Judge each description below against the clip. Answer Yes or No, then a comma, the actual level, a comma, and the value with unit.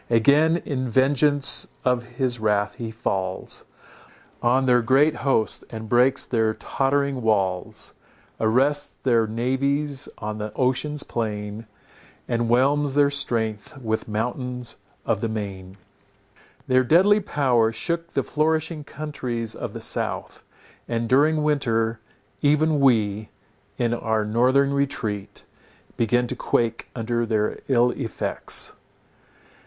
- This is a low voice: Yes, low, 125 Hz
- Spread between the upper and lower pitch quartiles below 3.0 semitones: No, average, 4.0 semitones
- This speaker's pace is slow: Yes, slow, 120 wpm